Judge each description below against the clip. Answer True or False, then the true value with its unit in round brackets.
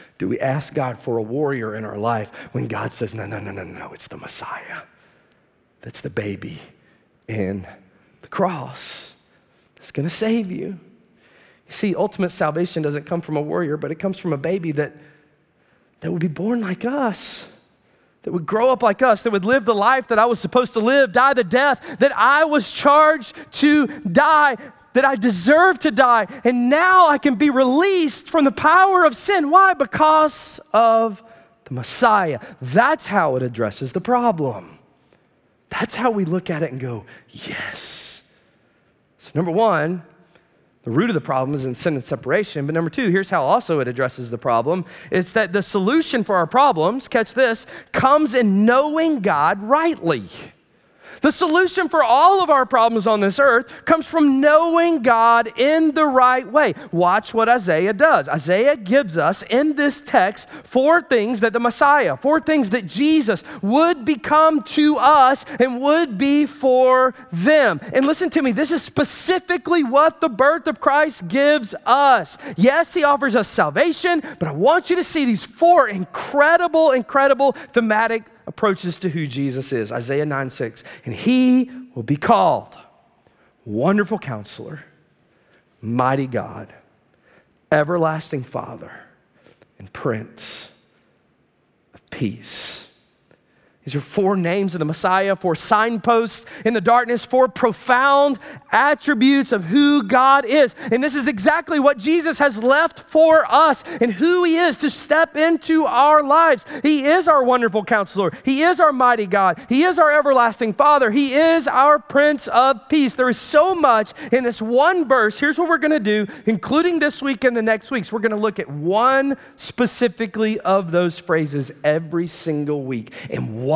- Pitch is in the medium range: False (245 Hz)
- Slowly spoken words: False (170 wpm)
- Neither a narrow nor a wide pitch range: False (8.2 semitones)